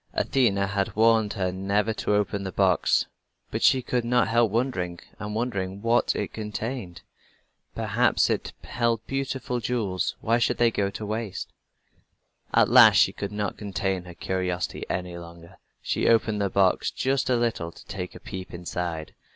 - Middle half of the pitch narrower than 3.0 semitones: No, average, 3.8 semitones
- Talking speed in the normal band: Yes, average, 165 wpm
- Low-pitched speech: Yes, low, 105 Hz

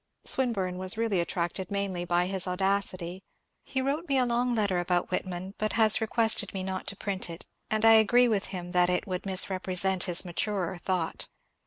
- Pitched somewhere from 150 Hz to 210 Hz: Yes, high, 190 Hz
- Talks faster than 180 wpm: Yes, average, 190 wpm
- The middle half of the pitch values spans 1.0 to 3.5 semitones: Yes, average, 3.1 semitones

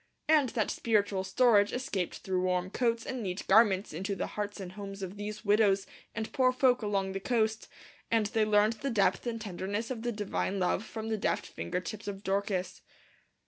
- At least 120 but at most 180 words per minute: No, average, 190 wpm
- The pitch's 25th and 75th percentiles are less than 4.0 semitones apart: Yes, average, 2.7 semitones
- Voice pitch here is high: Yes, high, 210 Hz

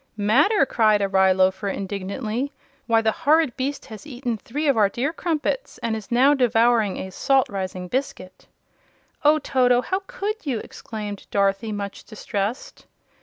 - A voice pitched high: Yes, high, 230 Hz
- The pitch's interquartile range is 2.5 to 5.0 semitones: No, wide, 5.5 semitones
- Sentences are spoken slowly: No, average, 155 wpm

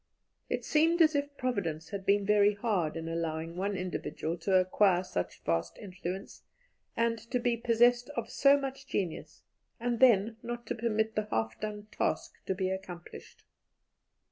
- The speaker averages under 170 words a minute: Yes, average, 160 wpm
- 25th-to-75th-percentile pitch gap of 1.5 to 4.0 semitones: No, average, 4.8 semitones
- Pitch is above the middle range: Yes, high, 205 Hz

